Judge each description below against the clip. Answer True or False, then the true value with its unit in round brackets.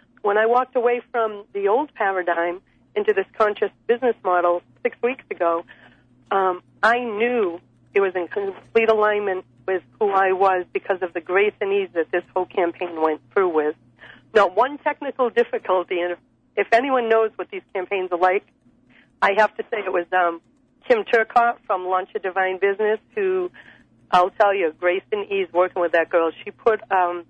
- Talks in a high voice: True (195 Hz)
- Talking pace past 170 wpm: True (180 wpm)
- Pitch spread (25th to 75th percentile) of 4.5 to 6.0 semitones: False (3.7 semitones)